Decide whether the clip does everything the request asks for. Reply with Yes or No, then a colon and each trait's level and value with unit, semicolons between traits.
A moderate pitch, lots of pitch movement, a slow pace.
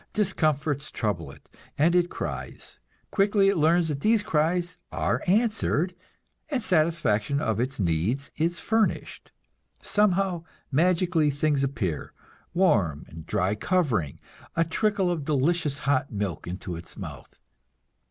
Yes: medium, 155 Hz; wide, 5.9 semitones; slow, 125 wpm